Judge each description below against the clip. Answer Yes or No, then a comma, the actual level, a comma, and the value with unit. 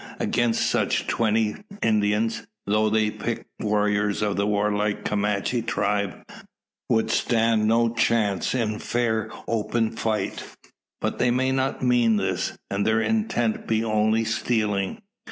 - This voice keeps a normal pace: No, slow, 130 wpm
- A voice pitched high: No, low, 110 Hz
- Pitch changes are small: Yes, narrow, 1.7 semitones